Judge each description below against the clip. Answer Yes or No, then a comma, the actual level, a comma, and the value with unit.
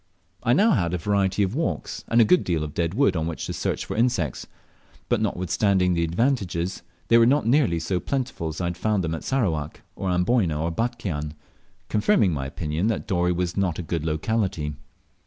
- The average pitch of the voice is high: No, very low, 90 Hz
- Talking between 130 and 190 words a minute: No, average, 200 wpm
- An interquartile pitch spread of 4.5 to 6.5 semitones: Yes, wide, 5.6 semitones